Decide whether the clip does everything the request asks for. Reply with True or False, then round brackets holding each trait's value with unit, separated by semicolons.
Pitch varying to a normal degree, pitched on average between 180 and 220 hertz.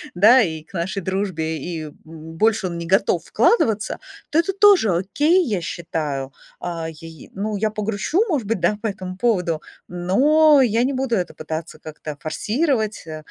False (6.0 semitones; 195 Hz)